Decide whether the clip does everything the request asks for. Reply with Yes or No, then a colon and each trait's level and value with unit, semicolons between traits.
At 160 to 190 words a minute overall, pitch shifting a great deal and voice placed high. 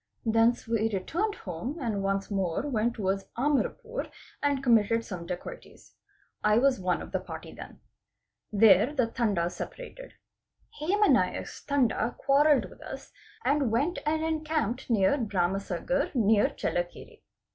No: slow, 135 wpm; wide, 6.5 semitones; high, 230 Hz